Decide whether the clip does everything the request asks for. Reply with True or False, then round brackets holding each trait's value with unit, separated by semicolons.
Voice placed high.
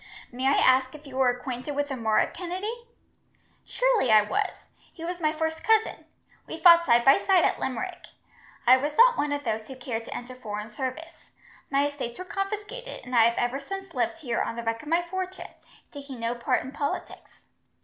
True (285 Hz)